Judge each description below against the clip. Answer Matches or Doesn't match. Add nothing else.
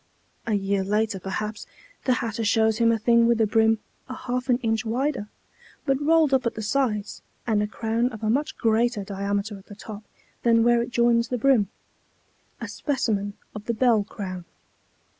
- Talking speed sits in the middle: Matches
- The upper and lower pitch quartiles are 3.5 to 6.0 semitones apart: Doesn't match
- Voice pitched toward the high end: Matches